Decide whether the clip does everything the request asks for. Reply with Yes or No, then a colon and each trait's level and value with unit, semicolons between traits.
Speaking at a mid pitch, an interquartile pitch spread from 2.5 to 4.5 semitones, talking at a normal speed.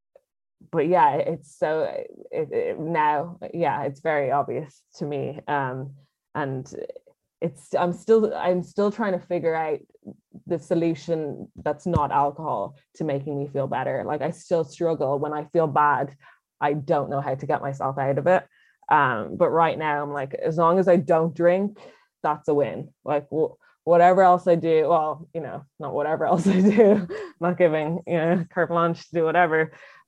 Yes: medium, 165 Hz; average, 3.9 semitones; average, 180 wpm